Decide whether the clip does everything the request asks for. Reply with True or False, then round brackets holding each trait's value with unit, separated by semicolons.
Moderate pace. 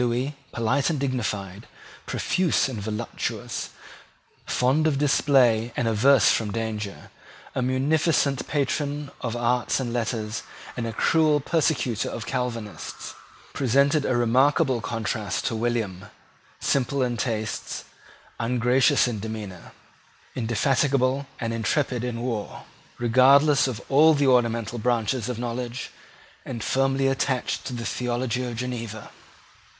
False (120 wpm)